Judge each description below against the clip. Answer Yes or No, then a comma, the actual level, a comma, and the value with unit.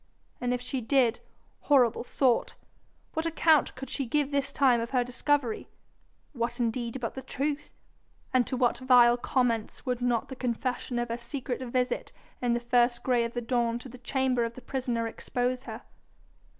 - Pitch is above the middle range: Yes, very high, 250 Hz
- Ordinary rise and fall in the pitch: No, narrow, 1.7 semitones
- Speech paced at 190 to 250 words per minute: No, average, 175 wpm